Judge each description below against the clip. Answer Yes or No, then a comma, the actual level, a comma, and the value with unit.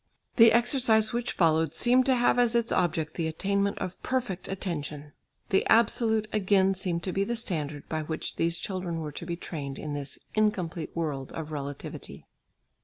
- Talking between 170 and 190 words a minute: Yes, average, 175 wpm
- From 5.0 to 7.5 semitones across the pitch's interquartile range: Yes, wide, 5.6 semitones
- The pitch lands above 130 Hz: Yes, medium, 185 Hz